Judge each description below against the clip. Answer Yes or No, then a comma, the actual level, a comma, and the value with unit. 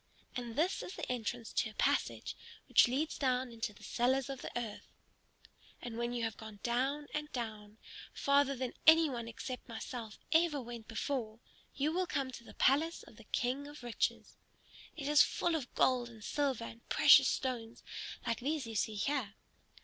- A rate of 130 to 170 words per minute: No, average, 180 wpm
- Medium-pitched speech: No, very high, 250 Hz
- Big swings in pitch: No, average, 3.7 semitones